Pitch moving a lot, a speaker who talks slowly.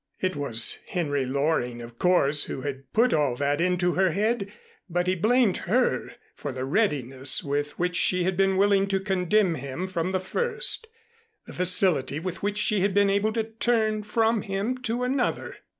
No: wide, 6.4 semitones; average, 180 wpm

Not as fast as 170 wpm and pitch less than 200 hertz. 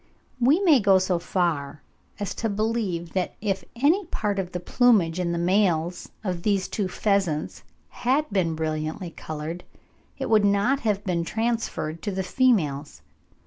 Yes: average, 155 wpm; high, 190 Hz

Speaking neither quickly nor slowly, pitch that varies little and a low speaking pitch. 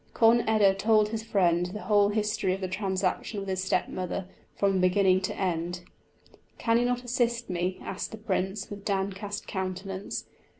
No: average, 170 wpm; narrow, 2.3 semitones; high, 195 Hz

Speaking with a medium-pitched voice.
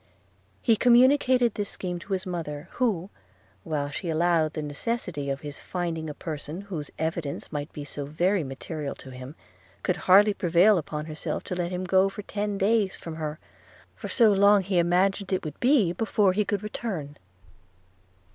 Yes: medium, 180 Hz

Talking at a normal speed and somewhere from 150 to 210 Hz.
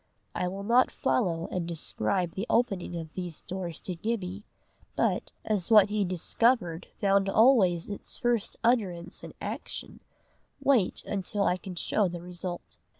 Yes: average, 150 wpm; high, 190 Hz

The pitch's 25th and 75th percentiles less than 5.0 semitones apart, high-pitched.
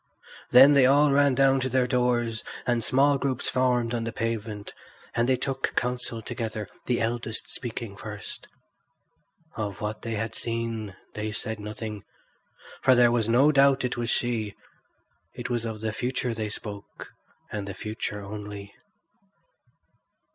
No: average, 2.8 semitones; low, 115 Hz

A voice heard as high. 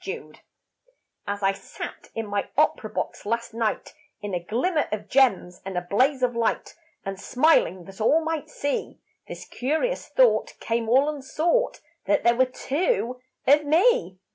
Yes: high, 245 Hz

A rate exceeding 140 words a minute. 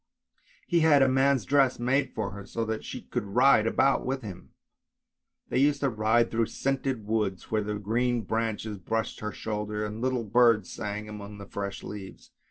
Yes: average, 180 wpm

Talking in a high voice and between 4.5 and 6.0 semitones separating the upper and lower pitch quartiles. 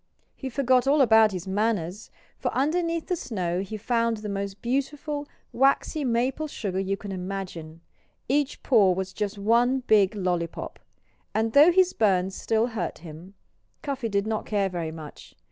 Yes: high, 215 Hz; wide, 5.5 semitones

